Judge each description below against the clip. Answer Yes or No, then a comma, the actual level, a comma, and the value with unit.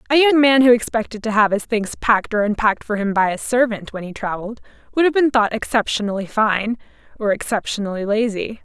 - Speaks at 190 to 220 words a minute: Yes, average, 200 wpm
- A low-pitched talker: No, high, 220 Hz